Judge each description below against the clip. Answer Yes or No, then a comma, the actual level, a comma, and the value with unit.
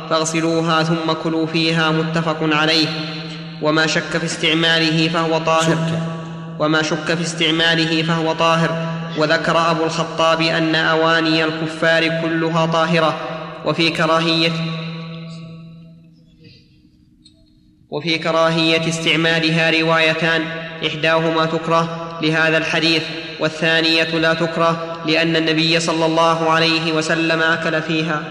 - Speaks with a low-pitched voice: No, medium, 165 Hz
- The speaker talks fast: No, average, 100 wpm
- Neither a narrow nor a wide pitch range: No, narrow, 0.4 semitones